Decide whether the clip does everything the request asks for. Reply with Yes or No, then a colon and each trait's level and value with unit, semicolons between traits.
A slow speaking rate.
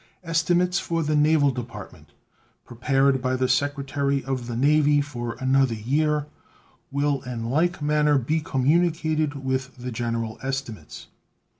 Yes: slow, 130 wpm